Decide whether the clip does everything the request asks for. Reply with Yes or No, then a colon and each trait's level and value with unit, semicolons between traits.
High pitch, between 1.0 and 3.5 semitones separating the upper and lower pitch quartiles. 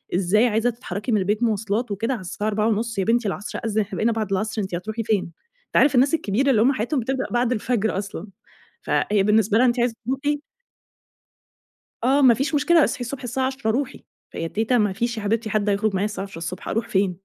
Yes: high, 220 Hz; average, 3.2 semitones